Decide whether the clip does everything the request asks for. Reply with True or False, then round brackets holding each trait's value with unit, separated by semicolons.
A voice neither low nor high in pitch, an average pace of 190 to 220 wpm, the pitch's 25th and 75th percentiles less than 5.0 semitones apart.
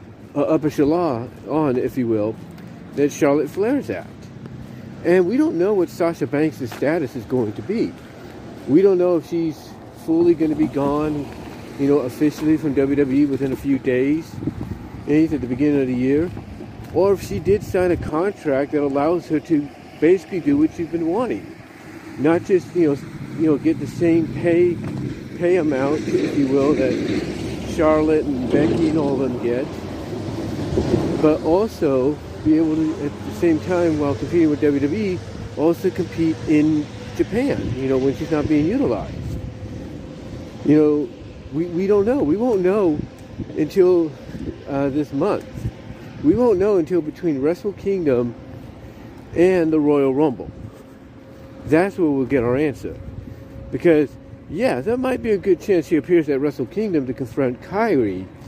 False (150 Hz; 160 wpm; 4.1 semitones)